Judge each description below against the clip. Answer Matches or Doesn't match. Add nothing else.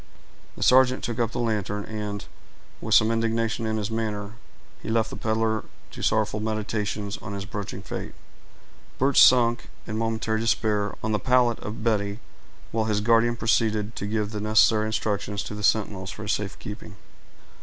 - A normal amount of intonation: Doesn't match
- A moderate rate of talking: Matches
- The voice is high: Doesn't match